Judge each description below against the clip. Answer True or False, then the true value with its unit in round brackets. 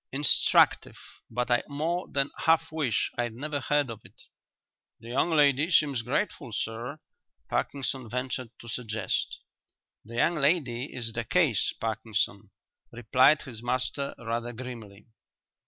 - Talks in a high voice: False (125 Hz)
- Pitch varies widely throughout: False (3.9 semitones)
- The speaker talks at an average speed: False (130 wpm)